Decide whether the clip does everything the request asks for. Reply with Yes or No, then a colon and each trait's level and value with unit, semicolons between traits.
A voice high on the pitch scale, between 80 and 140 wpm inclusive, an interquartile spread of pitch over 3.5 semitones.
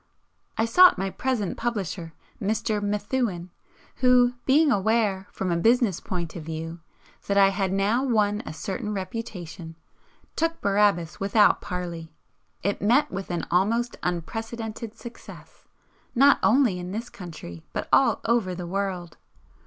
Yes: high, 200 Hz; slow, 135 wpm; average, 4.4 semitones